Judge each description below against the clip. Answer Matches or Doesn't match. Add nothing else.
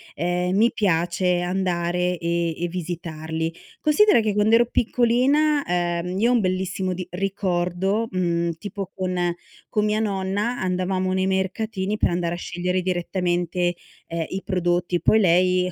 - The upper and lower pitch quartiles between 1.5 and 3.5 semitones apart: Matches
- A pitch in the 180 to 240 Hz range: Matches